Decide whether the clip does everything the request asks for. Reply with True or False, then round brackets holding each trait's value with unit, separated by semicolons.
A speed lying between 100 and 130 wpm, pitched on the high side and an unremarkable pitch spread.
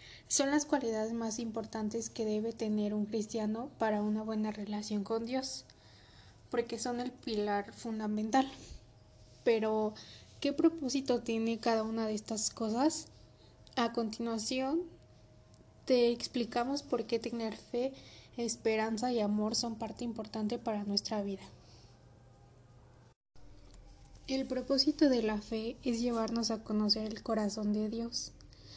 False (125 wpm; 225 Hz; 2.2 semitones)